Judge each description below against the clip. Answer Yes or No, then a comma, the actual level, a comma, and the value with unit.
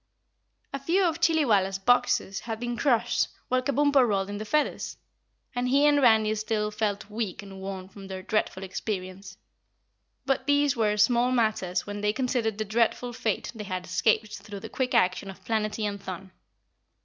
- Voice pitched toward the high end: Yes, high, 215 Hz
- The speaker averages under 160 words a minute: No, average, 175 wpm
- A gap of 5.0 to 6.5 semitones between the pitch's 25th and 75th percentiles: No, average, 4.0 semitones